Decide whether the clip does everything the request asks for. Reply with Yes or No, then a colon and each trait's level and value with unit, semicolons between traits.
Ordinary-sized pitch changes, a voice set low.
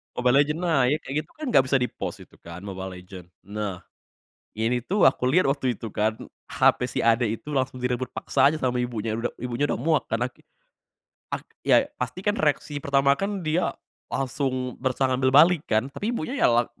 Yes: average, 4.0 semitones; low, 130 Hz